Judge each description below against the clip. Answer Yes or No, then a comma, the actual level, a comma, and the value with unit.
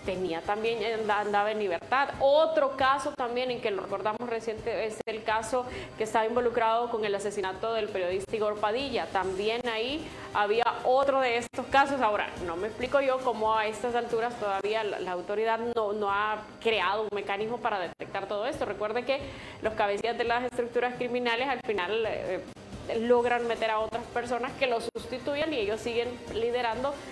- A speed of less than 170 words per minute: No, average, 175 wpm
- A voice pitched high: Yes, high, 230 Hz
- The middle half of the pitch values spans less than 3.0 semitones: Yes, narrow, 2.5 semitones